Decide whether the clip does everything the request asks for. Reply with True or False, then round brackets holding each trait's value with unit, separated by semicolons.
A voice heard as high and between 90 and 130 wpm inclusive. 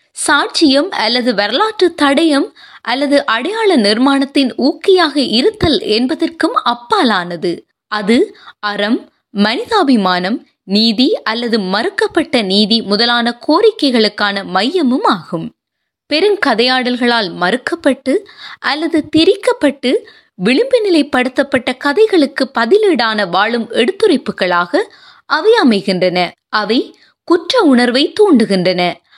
False (270 Hz; 80 wpm)